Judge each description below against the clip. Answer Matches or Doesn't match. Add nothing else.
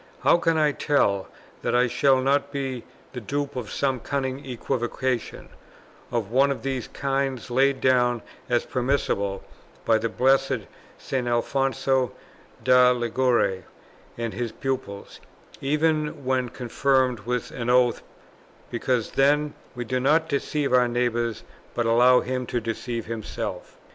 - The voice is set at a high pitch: Doesn't match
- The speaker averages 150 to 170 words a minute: Doesn't match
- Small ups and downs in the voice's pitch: Matches